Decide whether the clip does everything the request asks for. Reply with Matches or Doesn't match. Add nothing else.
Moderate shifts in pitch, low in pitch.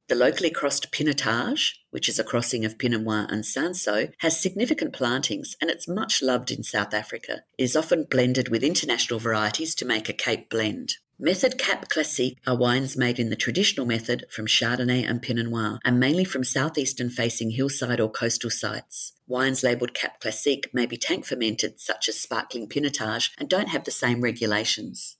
Matches